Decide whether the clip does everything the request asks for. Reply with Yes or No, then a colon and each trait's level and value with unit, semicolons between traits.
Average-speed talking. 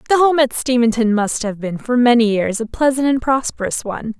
No: fast, 215 wpm